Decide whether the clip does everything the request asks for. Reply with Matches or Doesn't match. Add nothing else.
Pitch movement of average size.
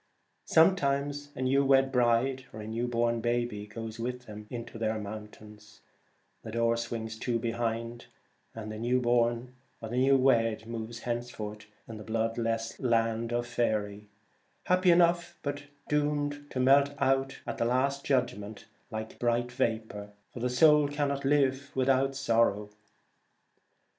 Matches